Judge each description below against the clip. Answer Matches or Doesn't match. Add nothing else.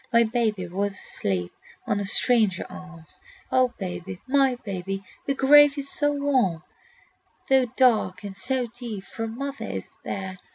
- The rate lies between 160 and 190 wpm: Doesn't match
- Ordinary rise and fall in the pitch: Doesn't match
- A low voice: Doesn't match